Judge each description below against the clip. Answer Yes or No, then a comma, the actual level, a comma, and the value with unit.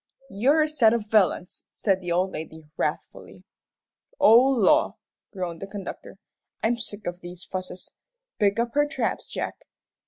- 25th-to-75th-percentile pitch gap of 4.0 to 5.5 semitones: Yes, average, 4.4 semitones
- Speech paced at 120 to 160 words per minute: Yes, average, 150 wpm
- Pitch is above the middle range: Yes, high, 205 Hz